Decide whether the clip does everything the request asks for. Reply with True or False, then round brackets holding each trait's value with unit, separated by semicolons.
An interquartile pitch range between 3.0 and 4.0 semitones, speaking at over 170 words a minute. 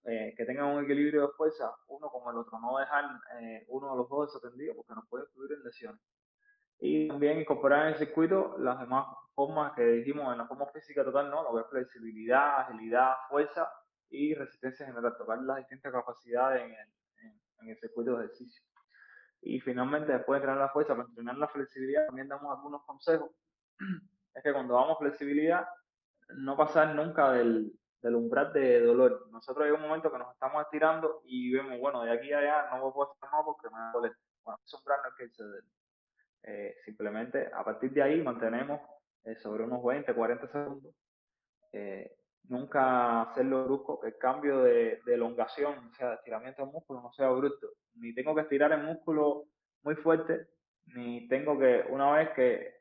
True (3.7 semitones; 185 wpm)